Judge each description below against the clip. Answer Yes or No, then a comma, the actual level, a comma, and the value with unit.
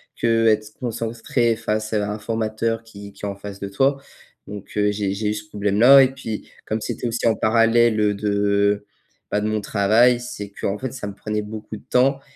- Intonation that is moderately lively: No, narrow, 2.0 semitones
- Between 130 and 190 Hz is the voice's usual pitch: No, low, 110 Hz